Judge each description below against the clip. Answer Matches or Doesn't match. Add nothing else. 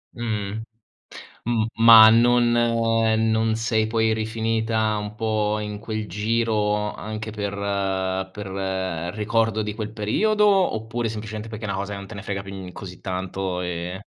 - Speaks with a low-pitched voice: Matches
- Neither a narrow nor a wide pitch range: Doesn't match